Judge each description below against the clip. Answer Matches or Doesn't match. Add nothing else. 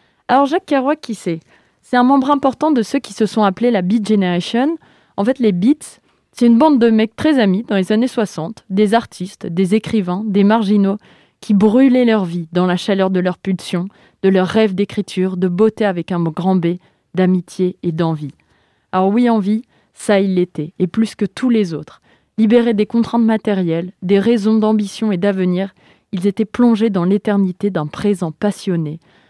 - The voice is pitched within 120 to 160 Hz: Doesn't match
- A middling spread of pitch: Matches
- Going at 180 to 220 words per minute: Matches